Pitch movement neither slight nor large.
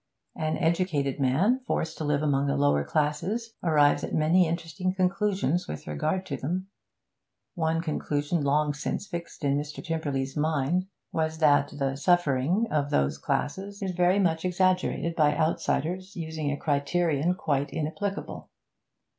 Yes: average, 3.9 semitones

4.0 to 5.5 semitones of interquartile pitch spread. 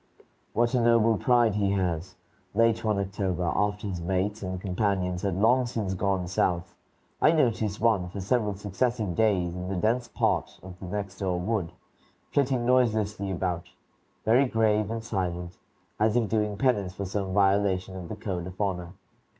No: average, 3.4 semitones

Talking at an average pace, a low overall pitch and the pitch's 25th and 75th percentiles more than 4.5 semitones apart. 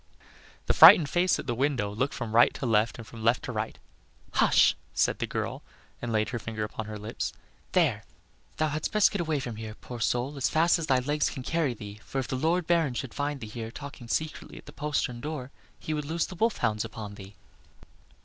No: fast, 225 wpm; low, 130 Hz; average, 5.1 semitones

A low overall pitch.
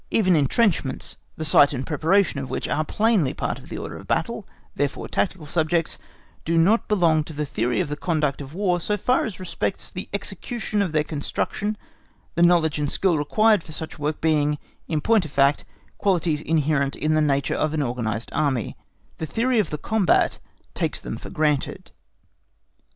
No: medium, 155 Hz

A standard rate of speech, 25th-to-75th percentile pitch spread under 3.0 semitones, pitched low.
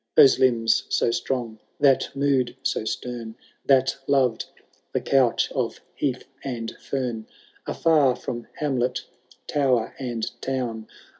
No: slow, 120 wpm; narrow, 2.6 semitones; low, 125 Hz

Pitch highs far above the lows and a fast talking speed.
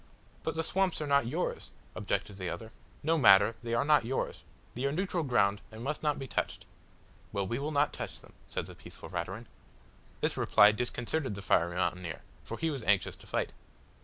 No: wide, 6.9 semitones; average, 195 wpm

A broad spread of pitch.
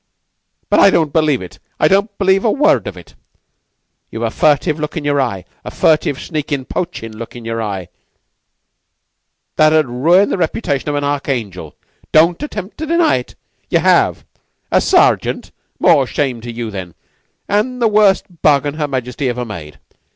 Yes: wide, 7.1 semitones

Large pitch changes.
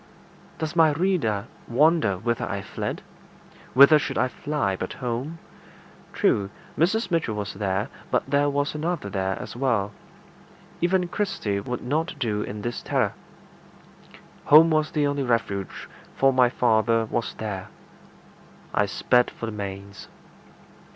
Yes: wide, 6.7 semitones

